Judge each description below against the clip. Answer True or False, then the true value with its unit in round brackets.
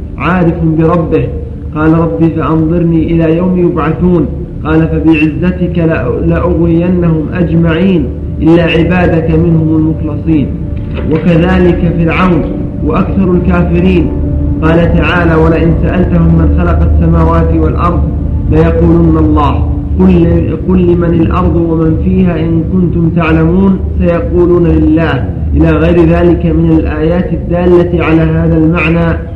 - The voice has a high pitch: False (160 Hz)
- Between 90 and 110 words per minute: True (105 wpm)